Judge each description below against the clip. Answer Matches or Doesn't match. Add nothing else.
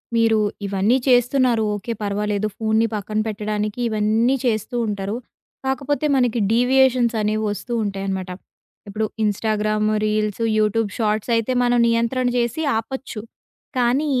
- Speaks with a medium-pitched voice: Doesn't match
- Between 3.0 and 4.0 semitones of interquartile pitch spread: Doesn't match